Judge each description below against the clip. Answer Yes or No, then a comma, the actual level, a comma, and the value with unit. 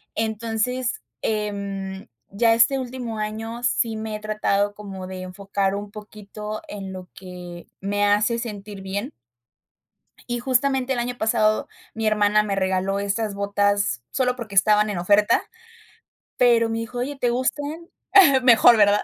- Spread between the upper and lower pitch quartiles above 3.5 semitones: No, average, 2.7 semitones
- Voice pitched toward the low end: No, high, 210 Hz